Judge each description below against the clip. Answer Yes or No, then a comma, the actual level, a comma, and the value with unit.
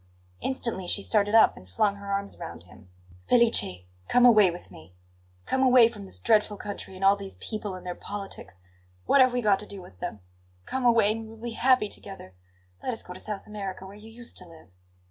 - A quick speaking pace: Yes, fast, 220 wpm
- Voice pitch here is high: Yes, high, 205 Hz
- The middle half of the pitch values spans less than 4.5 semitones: Yes, average, 3.3 semitones